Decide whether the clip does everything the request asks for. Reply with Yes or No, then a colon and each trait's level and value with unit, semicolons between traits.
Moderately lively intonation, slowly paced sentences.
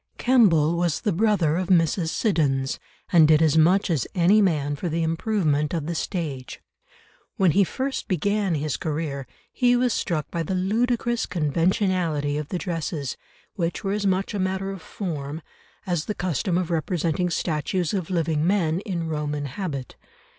No: average, 4.0 semitones; average, 165 wpm